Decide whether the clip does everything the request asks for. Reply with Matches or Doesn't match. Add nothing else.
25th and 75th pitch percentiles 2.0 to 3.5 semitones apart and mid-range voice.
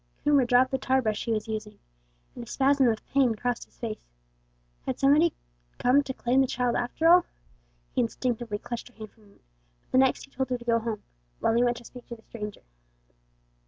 Doesn't match